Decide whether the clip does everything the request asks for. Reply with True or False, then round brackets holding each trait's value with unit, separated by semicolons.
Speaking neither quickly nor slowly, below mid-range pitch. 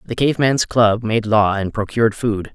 False (210 wpm; 115 Hz)